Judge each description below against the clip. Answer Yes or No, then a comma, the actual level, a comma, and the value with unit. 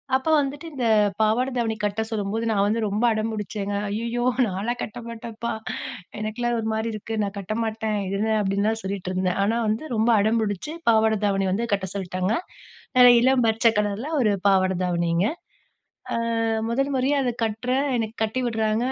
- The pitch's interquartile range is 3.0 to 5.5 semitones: No, narrow, 2.6 semitones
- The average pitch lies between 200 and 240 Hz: Yes, high, 220 Hz